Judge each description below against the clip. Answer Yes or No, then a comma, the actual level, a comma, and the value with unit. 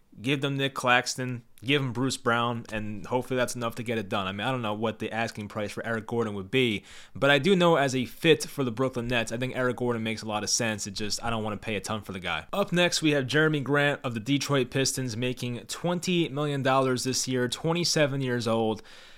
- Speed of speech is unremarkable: No, fast, 255 wpm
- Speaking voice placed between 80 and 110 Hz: No, low, 125 Hz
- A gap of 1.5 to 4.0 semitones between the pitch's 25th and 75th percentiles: Yes, average, 3.6 semitones